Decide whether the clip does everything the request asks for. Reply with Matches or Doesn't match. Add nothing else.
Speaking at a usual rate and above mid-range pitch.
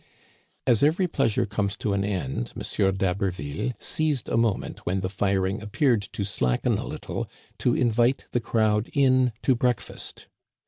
Doesn't match